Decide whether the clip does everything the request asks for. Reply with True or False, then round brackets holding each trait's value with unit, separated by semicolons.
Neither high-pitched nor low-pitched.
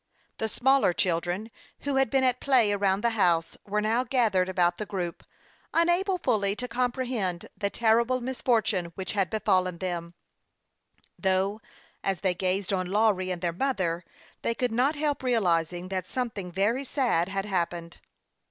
False (205 Hz)